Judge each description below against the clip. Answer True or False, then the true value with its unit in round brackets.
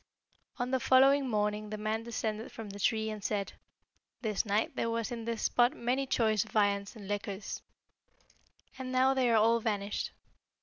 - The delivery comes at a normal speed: True (170 wpm)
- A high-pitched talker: True (220 Hz)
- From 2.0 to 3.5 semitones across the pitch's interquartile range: True (2.6 semitones)